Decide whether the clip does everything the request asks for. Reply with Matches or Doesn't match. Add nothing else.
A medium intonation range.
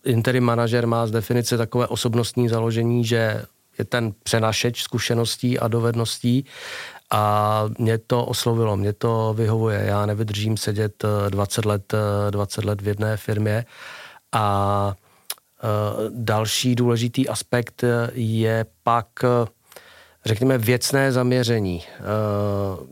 Doesn't match